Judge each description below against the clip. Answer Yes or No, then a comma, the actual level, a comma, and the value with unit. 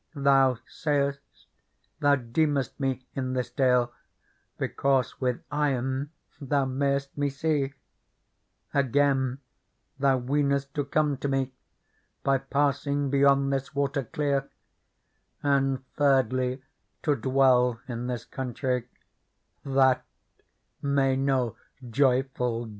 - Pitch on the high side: No, low, 135 Hz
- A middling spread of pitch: No, narrow, 1.5 semitones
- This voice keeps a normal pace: No, slow, 105 wpm